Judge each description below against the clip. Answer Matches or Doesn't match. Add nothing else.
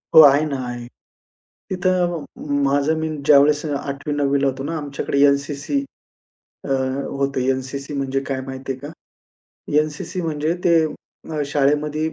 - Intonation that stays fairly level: Matches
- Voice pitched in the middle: Matches